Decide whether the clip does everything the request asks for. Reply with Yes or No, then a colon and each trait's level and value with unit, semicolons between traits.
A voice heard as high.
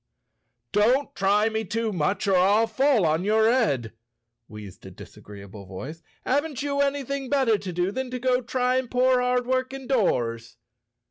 Yes: high, 225 Hz